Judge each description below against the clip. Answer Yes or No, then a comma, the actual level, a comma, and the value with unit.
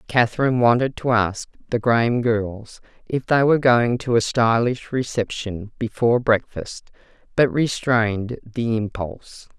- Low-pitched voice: Yes, low, 115 Hz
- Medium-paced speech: No, slow, 130 wpm